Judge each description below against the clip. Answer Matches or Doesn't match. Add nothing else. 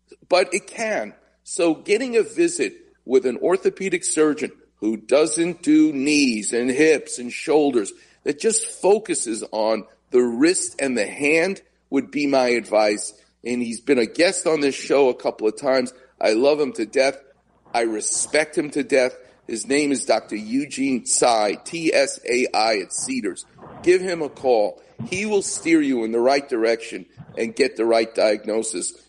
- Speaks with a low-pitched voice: Doesn't match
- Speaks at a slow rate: Doesn't match